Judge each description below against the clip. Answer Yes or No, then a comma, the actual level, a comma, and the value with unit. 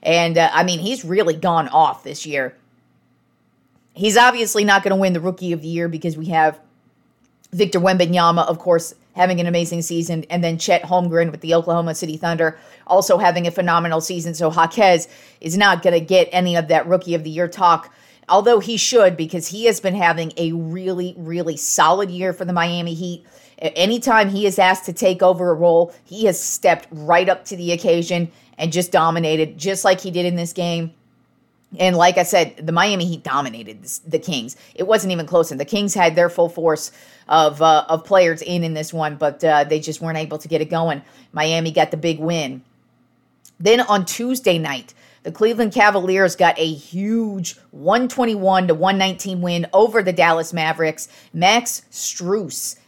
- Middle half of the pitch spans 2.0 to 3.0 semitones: Yes, narrow, 2.5 semitones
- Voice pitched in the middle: Yes, medium, 170 Hz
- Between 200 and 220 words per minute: No, average, 190 wpm